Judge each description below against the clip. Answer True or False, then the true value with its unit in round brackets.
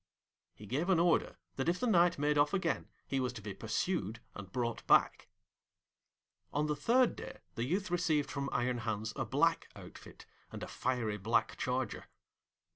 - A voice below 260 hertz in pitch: True (135 Hz)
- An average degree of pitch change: False (6.8 semitones)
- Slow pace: False (175 wpm)